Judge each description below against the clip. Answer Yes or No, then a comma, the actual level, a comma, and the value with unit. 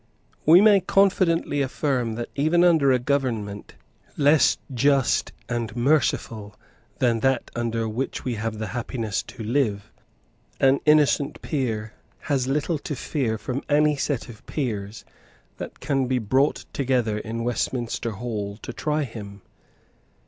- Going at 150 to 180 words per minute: No, slow, 135 wpm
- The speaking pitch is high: No, low, 125 Hz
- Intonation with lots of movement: No, average, 4.3 semitones